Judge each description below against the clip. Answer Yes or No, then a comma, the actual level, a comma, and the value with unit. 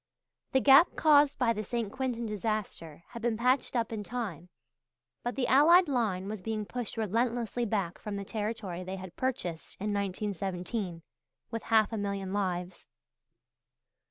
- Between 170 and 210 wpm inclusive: No, average, 155 wpm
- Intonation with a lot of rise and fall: No, average, 3.9 semitones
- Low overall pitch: No, high, 215 Hz